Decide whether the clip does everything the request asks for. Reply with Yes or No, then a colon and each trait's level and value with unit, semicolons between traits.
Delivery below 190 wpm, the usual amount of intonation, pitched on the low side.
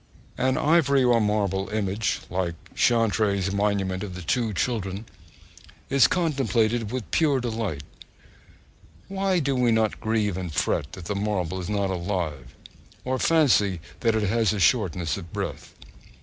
Yes: average, 145 wpm; average, 4.5 semitones; low, 105 Hz